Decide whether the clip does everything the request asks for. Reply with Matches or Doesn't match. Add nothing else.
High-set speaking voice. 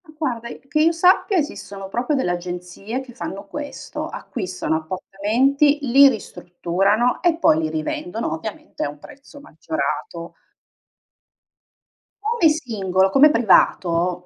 Matches